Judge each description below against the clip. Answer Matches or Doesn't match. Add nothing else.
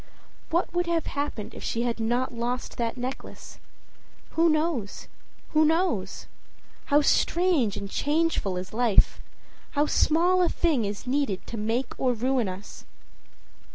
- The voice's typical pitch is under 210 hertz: Doesn't match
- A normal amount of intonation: Doesn't match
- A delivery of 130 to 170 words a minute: Matches